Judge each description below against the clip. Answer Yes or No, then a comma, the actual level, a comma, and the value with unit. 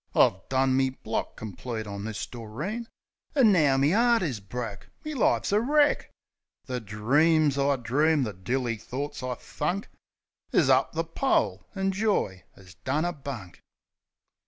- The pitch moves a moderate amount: No, wide, 7.5 semitones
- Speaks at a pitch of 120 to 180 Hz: Yes, low, 135 Hz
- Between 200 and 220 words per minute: No, average, 150 wpm